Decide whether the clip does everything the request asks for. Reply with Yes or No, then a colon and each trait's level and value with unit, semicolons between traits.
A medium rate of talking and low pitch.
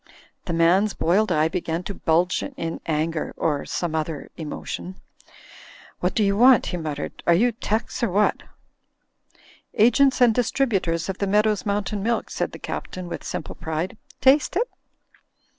No: average, 160 wpm; high, 190 Hz